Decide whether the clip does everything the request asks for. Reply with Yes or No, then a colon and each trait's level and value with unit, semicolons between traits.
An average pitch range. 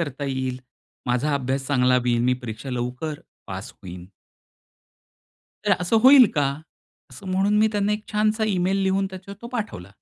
No: wide, 8.0 semitones